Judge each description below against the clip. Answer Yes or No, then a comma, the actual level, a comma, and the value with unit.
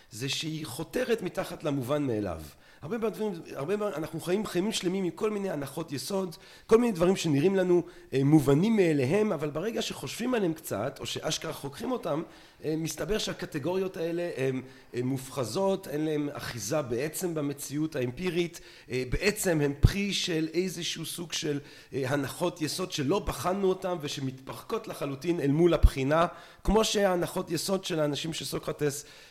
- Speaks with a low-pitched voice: No, medium, 165 Hz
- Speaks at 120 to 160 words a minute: Yes, average, 145 wpm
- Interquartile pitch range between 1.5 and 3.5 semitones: No, average, 4.4 semitones